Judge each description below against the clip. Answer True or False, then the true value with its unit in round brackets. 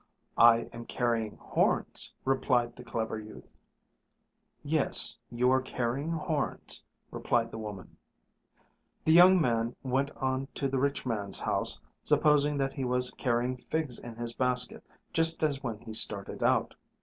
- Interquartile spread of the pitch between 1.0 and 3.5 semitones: True (2.9 semitones)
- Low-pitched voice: True (125 Hz)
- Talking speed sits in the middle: True (145 wpm)